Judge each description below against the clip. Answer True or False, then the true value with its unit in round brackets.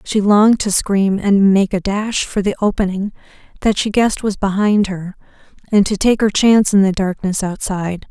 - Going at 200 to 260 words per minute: False (190 wpm)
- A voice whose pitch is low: False (200 Hz)